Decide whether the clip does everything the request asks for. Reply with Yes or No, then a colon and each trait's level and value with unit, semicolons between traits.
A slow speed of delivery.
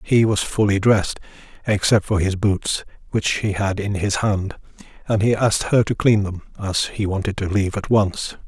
No: average, 200 wpm